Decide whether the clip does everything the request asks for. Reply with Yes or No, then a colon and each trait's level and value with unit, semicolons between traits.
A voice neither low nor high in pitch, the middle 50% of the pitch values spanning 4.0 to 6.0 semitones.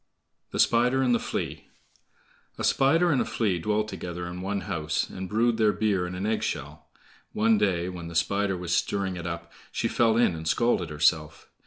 No: very low, 95 Hz; average, 4.3 semitones